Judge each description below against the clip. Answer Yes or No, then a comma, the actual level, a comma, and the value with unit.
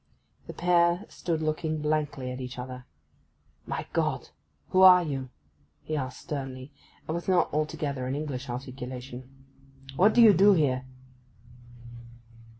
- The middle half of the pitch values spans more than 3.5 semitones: Yes, average, 4.9 semitones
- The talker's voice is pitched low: No, medium, 145 Hz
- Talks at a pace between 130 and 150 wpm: Yes, slow, 135 wpm